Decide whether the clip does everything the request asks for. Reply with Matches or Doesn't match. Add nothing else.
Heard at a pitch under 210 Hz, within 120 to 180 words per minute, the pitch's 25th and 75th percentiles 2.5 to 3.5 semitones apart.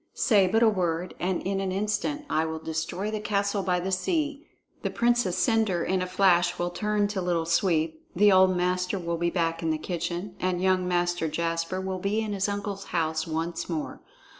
Doesn't match